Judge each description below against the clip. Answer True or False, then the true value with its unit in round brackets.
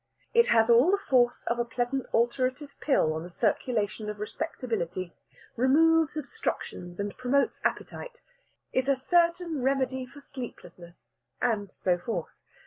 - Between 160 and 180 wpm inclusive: False (135 wpm)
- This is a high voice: True (250 Hz)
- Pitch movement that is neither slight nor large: True (4.8 semitones)